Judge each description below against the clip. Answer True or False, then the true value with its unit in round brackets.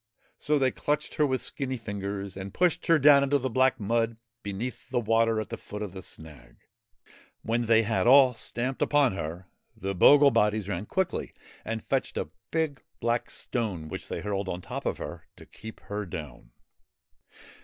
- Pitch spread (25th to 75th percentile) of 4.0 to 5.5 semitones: True (5.0 semitones)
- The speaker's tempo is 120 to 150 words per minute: False (180 wpm)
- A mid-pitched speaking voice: False (115 Hz)